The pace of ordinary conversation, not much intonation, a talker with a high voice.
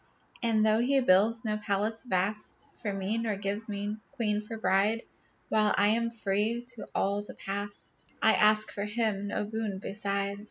Yes: average, 170 wpm; narrow, 1.9 semitones; high, 210 Hz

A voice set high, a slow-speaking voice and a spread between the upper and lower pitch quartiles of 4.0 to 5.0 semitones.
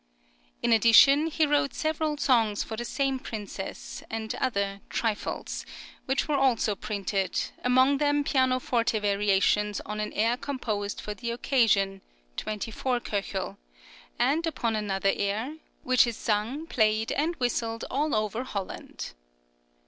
Yes: high, 230 Hz; slow, 130 wpm; average, 4.3 semitones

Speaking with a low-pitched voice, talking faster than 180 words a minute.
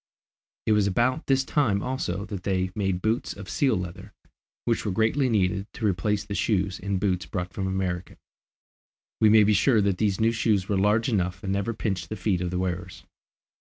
Yes: low, 100 Hz; average, 195 wpm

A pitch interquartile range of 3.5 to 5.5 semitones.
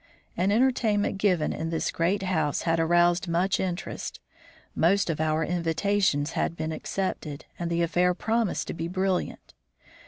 No: average, 2.9 semitones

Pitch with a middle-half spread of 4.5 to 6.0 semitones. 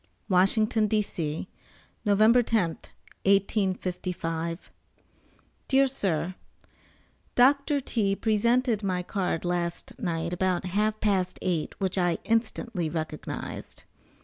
No: average, 3.8 semitones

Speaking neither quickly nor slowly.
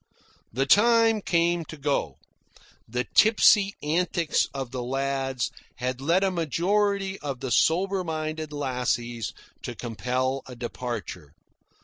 No: slow, 120 wpm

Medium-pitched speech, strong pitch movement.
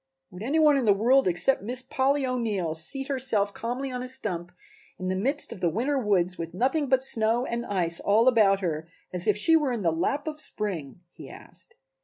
No: high, 225 Hz; wide, 6.2 semitones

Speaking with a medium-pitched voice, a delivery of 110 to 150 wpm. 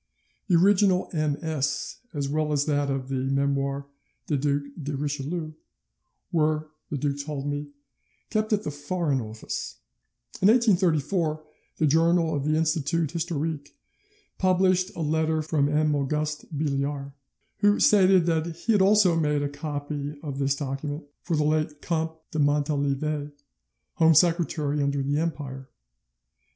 Yes: medium, 150 Hz; average, 140 wpm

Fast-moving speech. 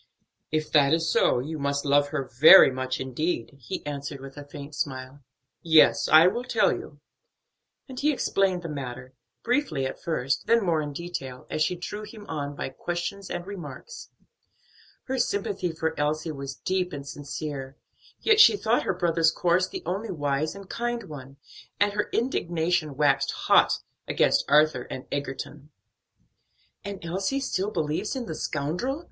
No: average, 165 wpm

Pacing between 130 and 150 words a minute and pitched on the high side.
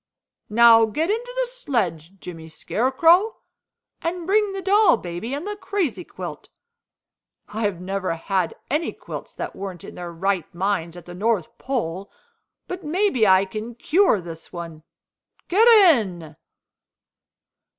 Yes: average, 140 wpm; high, 220 Hz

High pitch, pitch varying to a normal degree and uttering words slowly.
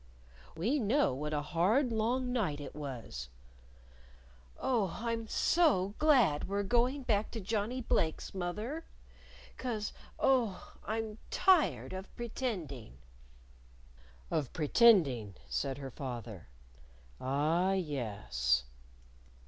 No: high, 195 Hz; wide, 8.6 semitones; slow, 105 wpm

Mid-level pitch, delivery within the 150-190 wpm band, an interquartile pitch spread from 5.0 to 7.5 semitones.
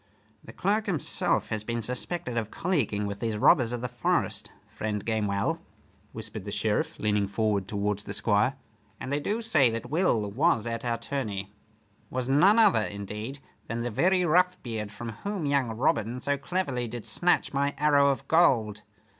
No: low, 120 Hz; average, 170 wpm; average, 5.3 semitones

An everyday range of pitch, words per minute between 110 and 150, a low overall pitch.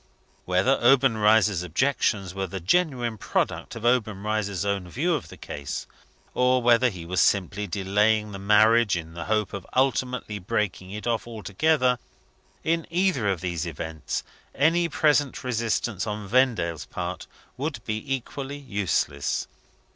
Yes: average, 4.9 semitones; average, 140 wpm; low, 110 Hz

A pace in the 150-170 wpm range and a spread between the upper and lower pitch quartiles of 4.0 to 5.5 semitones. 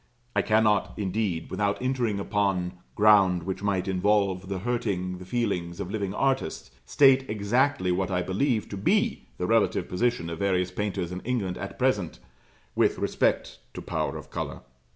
No: average, 160 wpm; average, 3.3 semitones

